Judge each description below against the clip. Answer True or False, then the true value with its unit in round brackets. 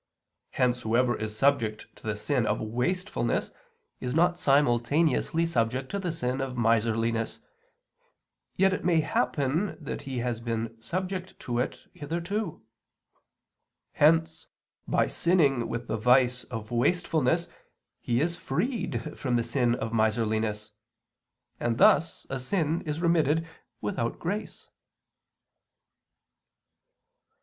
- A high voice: False (130 Hz)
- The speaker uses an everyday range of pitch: False (6.1 semitones)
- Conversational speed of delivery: False (120 wpm)